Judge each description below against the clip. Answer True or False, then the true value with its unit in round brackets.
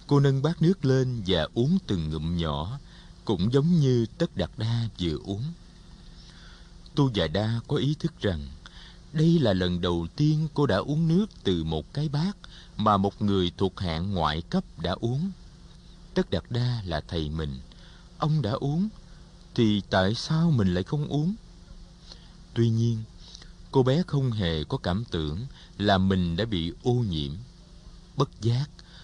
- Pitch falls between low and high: False (115 Hz)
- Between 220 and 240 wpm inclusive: False (165 wpm)